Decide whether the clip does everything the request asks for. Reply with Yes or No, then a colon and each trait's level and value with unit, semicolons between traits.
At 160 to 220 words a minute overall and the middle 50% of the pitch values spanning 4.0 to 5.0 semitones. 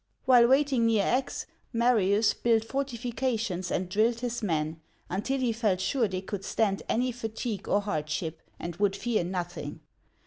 No: average, 150 wpm; average, 4.4 semitones